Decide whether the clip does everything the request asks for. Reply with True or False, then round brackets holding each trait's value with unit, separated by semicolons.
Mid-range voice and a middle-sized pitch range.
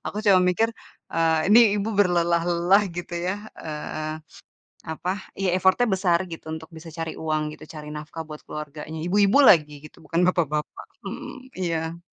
True (170 Hz; 3.3 semitones)